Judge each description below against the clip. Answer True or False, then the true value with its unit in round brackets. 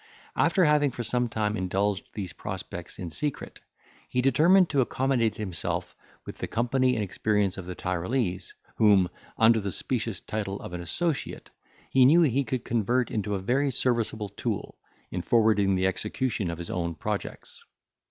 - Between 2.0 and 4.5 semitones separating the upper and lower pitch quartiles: False (5.0 semitones)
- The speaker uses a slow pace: False (160 wpm)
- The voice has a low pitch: True (110 Hz)